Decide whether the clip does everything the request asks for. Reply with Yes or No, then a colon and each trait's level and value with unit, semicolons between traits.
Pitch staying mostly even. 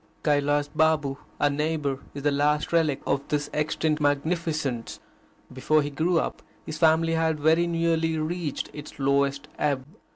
Yes: narrow, 2.0 semitones